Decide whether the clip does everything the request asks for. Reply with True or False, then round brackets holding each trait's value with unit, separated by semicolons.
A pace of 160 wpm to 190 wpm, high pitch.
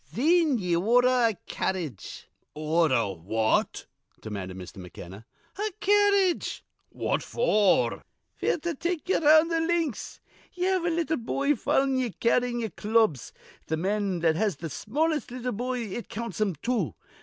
False (150 wpm; 235 Hz)